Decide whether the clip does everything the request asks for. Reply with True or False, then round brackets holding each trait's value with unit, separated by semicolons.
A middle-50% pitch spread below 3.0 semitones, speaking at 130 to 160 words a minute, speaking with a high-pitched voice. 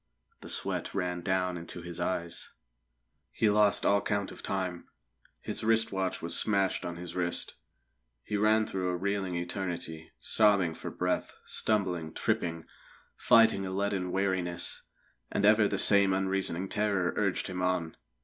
False (2.4 semitones; 150 wpm; 95 Hz)